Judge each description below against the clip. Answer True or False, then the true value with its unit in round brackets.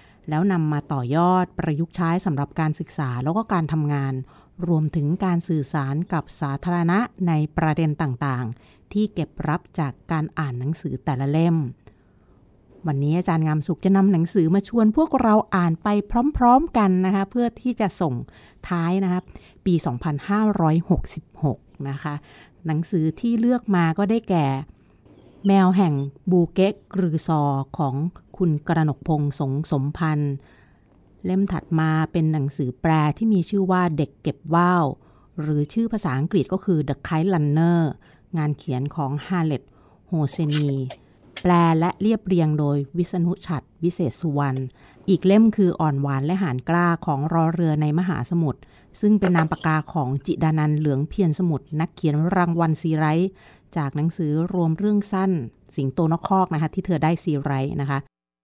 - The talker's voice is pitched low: False (160 Hz)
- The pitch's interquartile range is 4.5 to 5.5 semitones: False (3.7 semitones)